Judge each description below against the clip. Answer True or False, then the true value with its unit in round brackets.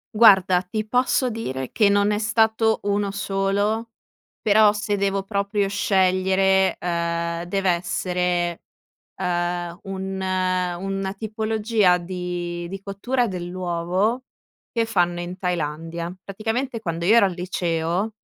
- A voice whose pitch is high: True (195 Hz)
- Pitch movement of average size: True (3.1 semitones)